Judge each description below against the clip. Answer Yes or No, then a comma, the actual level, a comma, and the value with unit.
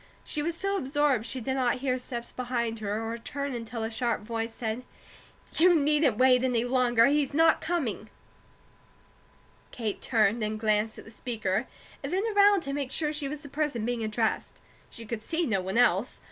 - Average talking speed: Yes, average, 190 wpm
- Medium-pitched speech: No, high, 245 Hz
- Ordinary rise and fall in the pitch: Yes, average, 4.3 semitones